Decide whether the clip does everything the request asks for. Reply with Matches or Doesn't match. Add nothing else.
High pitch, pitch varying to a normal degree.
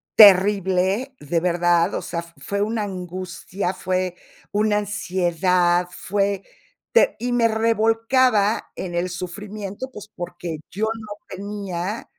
Matches